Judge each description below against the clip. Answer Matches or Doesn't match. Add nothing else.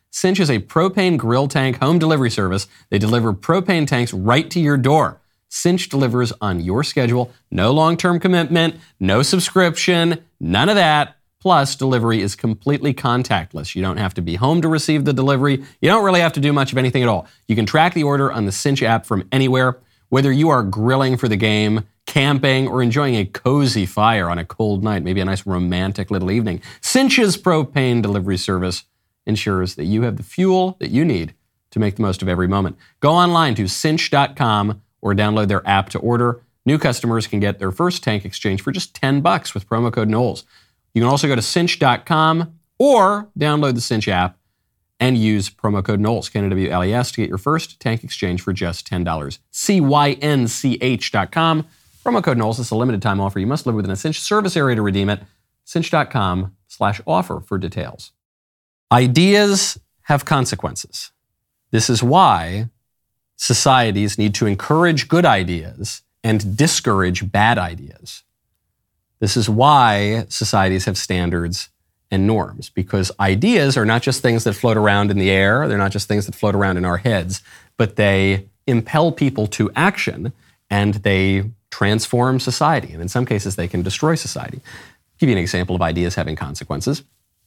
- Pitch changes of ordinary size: Doesn't match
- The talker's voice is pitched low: Matches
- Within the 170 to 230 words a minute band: Matches